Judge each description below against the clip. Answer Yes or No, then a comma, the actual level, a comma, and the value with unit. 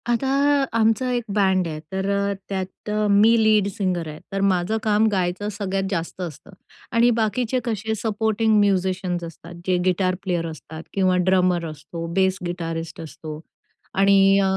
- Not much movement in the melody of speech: No, average, 3.1 semitones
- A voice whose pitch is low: No, high, 190 Hz